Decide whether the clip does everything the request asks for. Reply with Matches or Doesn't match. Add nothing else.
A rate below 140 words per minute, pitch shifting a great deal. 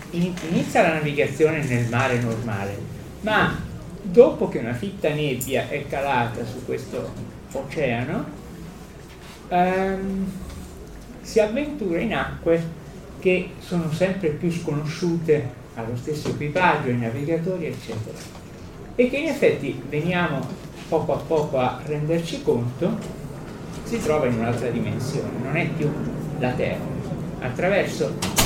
Matches